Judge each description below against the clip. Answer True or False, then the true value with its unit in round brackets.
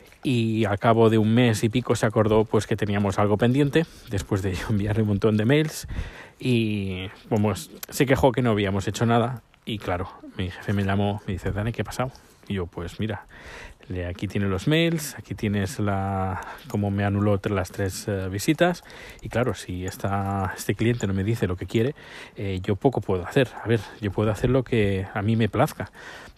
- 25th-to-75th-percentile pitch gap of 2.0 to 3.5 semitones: True (3.0 semitones)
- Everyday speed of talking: False (200 wpm)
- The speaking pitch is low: True (105 Hz)